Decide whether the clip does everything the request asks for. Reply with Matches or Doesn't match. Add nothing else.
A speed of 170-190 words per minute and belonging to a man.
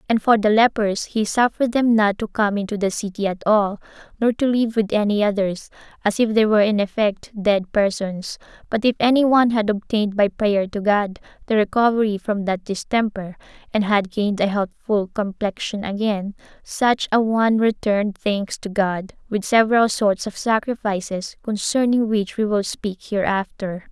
Doesn't match